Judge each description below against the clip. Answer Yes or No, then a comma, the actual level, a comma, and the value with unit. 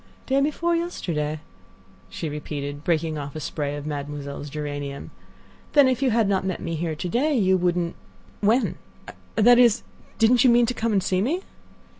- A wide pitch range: Yes, wide, 8.3 semitones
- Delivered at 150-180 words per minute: Yes, average, 165 wpm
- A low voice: No, medium, 180 Hz